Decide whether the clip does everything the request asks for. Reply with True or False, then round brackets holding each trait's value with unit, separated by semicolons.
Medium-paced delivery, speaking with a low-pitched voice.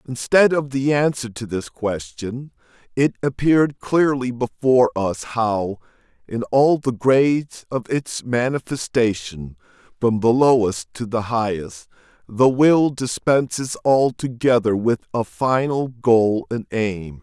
False (125 wpm; 125 Hz)